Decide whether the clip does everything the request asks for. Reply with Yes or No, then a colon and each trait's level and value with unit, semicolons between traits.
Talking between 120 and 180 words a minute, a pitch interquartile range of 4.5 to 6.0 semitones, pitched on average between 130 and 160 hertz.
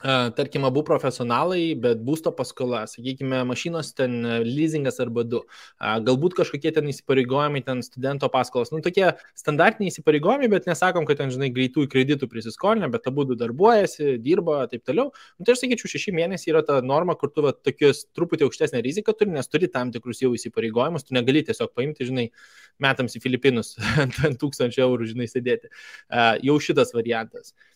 Yes: average, 170 wpm; average, 5.0 semitones; medium, 140 Hz